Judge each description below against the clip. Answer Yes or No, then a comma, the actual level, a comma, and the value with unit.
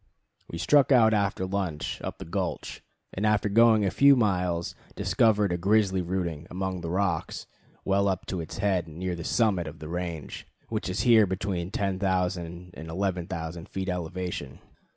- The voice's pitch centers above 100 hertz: No, very low, 95 Hz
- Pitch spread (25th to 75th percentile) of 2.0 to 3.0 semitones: Yes, average, 2.7 semitones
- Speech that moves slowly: No, average, 165 wpm